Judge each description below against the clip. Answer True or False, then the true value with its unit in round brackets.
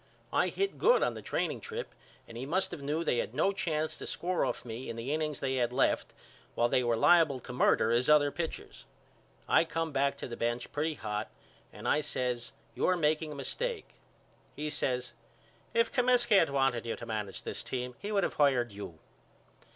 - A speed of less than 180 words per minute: False (200 wpm)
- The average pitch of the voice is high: False (140 Hz)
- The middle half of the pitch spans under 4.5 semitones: False (5.3 semitones)